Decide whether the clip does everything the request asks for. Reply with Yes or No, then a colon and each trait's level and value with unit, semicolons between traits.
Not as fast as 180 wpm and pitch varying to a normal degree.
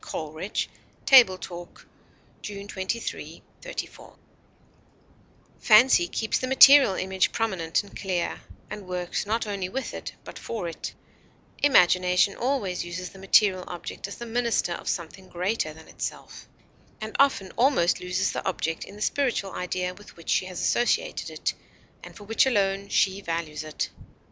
Yes: average, 150 wpm; average, 3.7 semitones